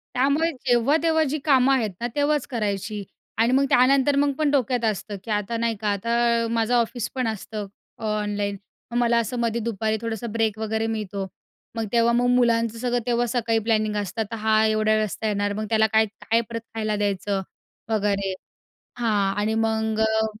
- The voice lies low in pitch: No, high, 225 Hz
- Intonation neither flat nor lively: No, narrow, 2.0 semitones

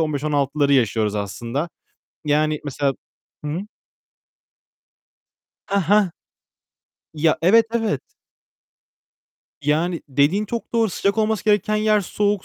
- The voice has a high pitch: No, medium, 160 Hz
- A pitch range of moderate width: No, wide, 6.6 semitones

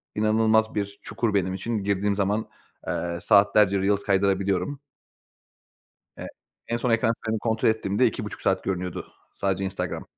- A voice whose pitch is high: No, low, 100 Hz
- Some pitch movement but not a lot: No, narrow, 2.3 semitones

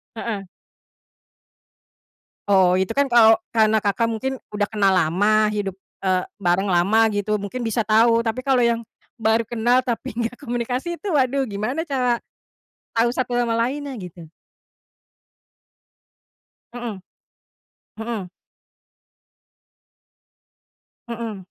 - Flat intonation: No, average, 3.0 semitones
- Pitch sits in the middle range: No, high, 225 Hz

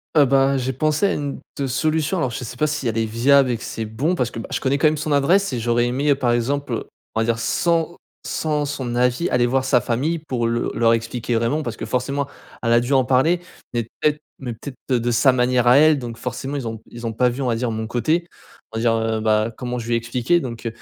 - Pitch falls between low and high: No, low, 125 Hz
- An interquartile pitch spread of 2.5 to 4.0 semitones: Yes, average, 3.4 semitones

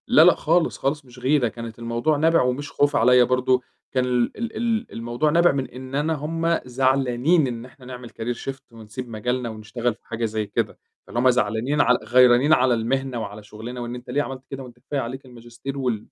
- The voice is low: Yes, low, 125 Hz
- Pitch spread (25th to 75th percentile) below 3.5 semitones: Yes, average, 2.7 semitones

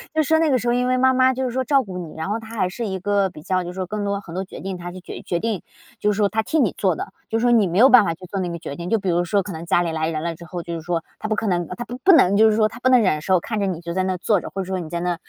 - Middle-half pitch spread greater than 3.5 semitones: Yes, average, 4.4 semitones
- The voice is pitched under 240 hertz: Yes, high, 195 Hz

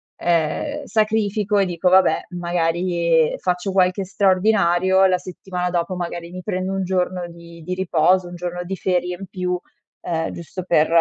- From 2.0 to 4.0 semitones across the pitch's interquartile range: No, narrow, 1.6 semitones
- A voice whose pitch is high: No, medium, 180 Hz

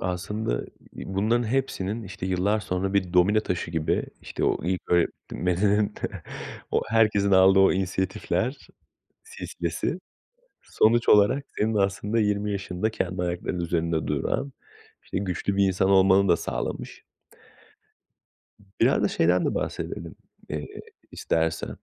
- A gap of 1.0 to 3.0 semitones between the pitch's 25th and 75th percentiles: Yes, average, 2.7 semitones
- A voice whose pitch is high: No, very low, 95 Hz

